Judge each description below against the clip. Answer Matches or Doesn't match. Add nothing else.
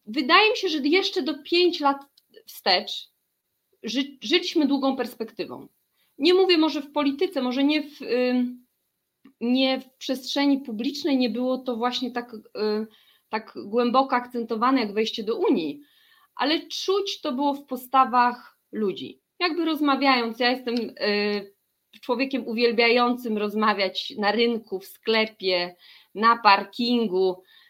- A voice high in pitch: Matches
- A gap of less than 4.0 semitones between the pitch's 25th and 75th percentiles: Doesn't match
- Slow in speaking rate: Doesn't match